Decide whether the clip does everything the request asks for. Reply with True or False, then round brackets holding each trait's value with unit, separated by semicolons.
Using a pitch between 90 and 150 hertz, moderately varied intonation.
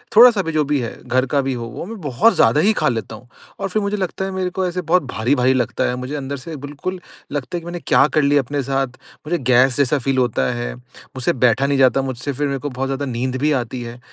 True (135 Hz; 4.5 semitones)